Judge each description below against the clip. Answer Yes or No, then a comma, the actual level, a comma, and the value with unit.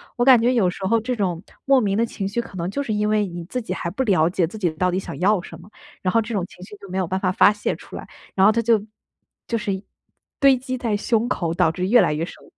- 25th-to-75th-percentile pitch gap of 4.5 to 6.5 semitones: No, average, 4.1 semitones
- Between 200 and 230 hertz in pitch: Yes, high, 205 Hz